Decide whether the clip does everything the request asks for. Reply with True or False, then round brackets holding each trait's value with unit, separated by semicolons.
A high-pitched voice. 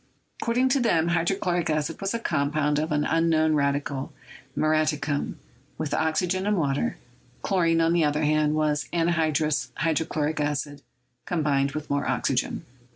False (155 Hz)